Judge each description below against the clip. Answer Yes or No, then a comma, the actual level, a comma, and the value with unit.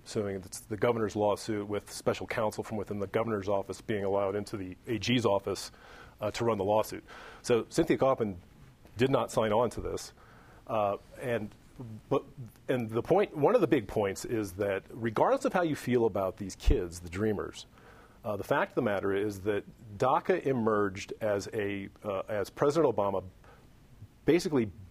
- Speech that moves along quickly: No, average, 175 wpm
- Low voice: Yes, low, 105 Hz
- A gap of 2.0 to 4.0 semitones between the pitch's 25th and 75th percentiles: Yes, average, 2.9 semitones